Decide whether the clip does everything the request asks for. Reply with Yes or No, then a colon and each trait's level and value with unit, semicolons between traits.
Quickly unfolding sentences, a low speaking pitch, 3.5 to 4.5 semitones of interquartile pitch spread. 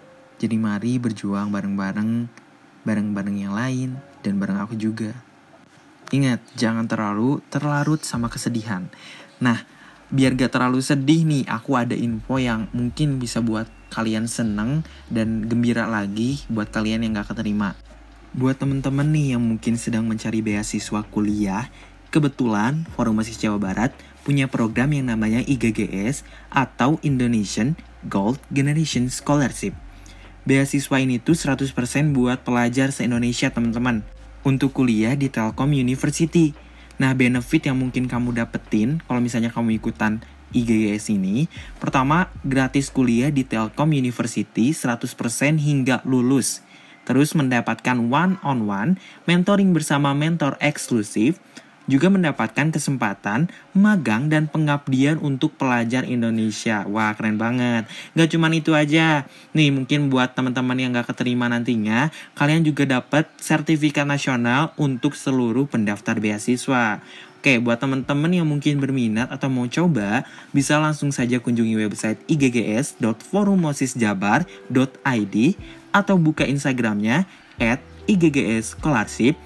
No: average, 120 wpm; low, 125 Hz; average, 4.2 semitones